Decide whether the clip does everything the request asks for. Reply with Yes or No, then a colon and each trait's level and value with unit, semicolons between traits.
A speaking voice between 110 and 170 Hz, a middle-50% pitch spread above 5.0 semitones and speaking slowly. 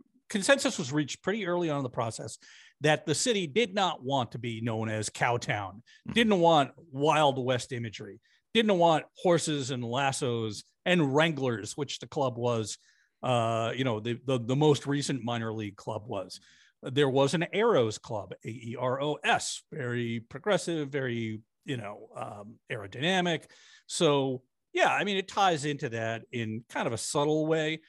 No: medium, 140 Hz; wide, 5.5 semitones; average, 160 wpm